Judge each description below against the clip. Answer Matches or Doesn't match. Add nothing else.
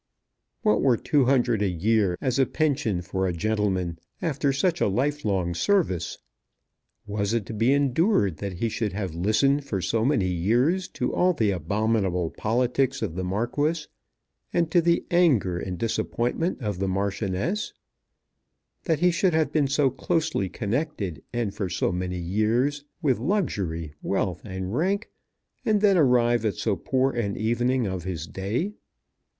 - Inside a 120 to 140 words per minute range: Doesn't match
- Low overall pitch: Matches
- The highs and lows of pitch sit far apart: Matches